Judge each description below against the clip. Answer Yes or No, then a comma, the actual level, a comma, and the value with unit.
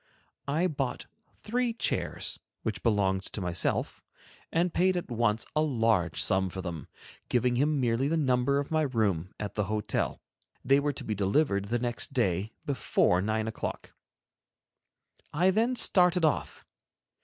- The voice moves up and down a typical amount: No, wide, 6.9 semitones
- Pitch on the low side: Yes, low, 120 Hz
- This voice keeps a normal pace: Yes, average, 150 wpm